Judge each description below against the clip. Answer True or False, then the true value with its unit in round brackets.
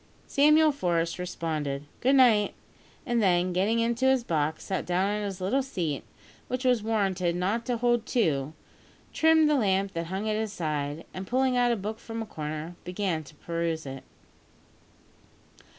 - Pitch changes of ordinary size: False (6.1 semitones)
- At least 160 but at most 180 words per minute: True (165 wpm)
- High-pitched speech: True (195 Hz)